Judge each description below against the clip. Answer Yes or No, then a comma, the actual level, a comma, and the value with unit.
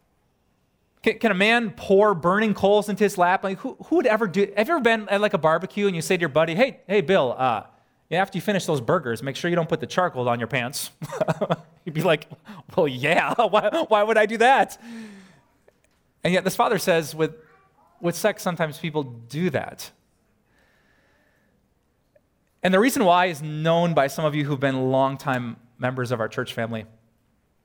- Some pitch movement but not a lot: No, wide, 6.4 semitones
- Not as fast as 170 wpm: No, average, 195 wpm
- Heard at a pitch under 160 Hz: No, medium, 175 Hz